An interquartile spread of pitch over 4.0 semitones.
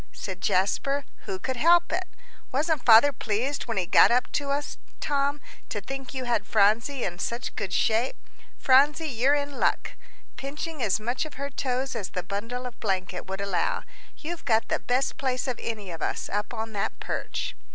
Yes: average, 5.2 semitones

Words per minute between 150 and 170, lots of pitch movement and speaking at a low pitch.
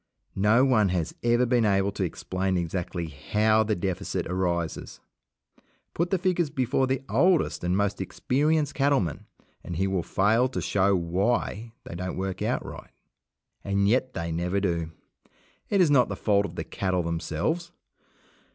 Yes: average, 160 wpm; wide, 6.1 semitones; low, 100 Hz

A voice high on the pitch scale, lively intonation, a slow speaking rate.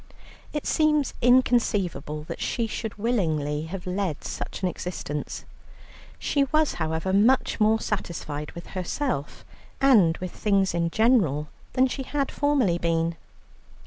Yes: high, 195 Hz; wide, 7.2 semitones; slow, 130 wpm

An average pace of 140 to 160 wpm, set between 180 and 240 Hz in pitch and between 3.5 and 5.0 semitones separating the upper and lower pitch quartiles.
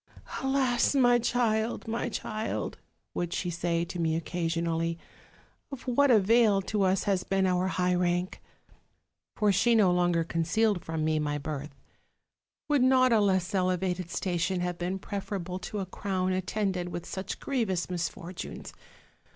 Yes: average, 150 wpm; medium, 185 Hz; average, 3.8 semitones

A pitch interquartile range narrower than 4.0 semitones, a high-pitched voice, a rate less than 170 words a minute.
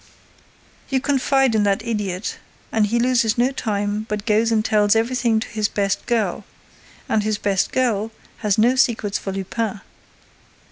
Yes: narrow, 2.4 semitones; high, 220 Hz; average, 155 wpm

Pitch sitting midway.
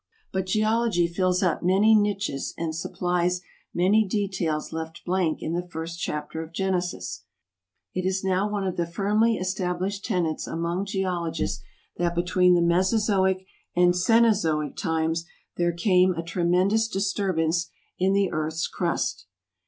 Yes: medium, 180 Hz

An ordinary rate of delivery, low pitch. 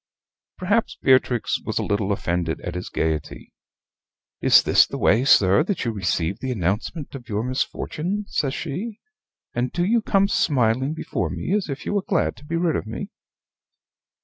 Yes: average, 175 wpm; low, 130 Hz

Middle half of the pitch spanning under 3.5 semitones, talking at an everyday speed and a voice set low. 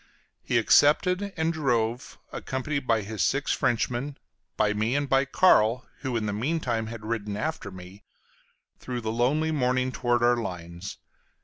No: average, 4.3 semitones; average, 155 wpm; low, 120 Hz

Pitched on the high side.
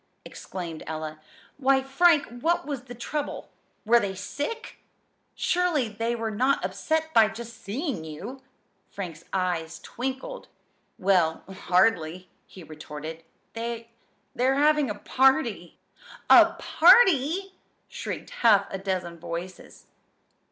Yes: high, 225 Hz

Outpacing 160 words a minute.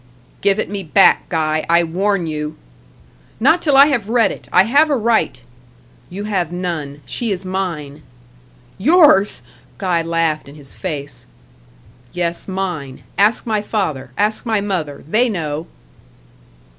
No: average, 145 wpm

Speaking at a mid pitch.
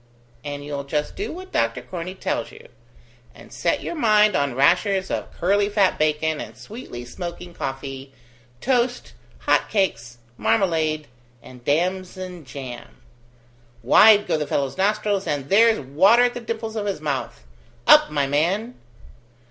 Yes: medium, 175 Hz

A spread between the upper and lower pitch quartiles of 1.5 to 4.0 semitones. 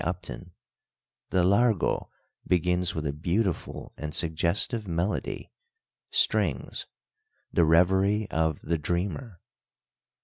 Yes: average, 3.1 semitones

